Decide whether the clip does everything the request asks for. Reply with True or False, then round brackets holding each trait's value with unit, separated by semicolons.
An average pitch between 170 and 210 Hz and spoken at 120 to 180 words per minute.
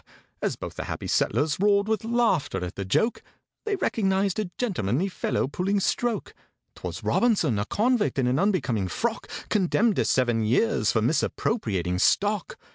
True (190 Hz; 150 wpm)